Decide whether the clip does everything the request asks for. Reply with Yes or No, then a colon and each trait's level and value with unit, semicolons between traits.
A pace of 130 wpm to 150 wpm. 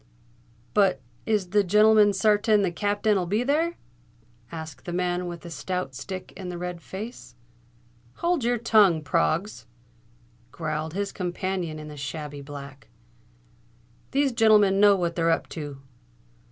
Yes: average, 140 wpm